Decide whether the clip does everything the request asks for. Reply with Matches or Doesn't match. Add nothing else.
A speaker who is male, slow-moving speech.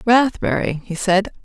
Doesn't match